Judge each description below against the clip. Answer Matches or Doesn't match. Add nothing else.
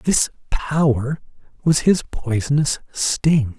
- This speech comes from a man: Matches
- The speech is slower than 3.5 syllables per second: Matches